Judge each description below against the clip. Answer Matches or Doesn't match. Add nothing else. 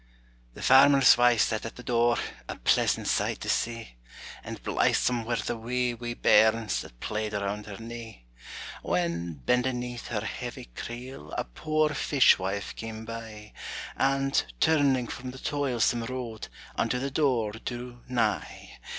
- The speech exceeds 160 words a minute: Doesn't match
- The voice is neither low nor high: Doesn't match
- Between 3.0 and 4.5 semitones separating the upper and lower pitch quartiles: Doesn't match